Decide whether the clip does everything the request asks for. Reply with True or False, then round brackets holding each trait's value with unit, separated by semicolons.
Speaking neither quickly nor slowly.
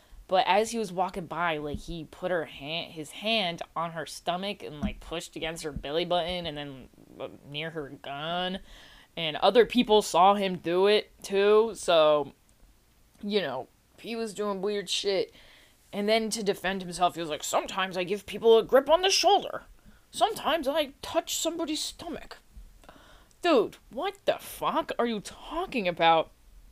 True (165 wpm)